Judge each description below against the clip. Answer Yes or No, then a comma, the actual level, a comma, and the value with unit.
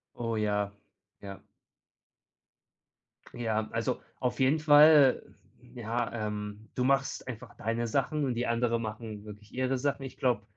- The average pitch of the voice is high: No, low, 115 Hz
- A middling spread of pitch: Yes, average, 3.4 semitones